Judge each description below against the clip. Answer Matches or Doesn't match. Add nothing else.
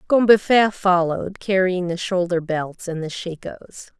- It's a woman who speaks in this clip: Matches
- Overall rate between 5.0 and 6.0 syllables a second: Doesn't match